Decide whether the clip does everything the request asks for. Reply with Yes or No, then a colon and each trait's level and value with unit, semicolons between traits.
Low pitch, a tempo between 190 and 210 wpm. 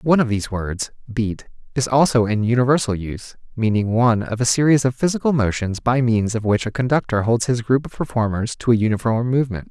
Yes: low, 120 Hz; fast, 205 wpm